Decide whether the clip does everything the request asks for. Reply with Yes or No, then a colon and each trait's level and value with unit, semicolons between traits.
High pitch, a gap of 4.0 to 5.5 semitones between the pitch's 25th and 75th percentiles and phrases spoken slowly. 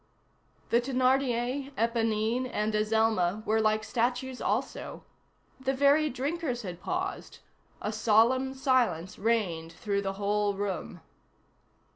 No: high, 230 Hz; average, 3.6 semitones; slow, 110 wpm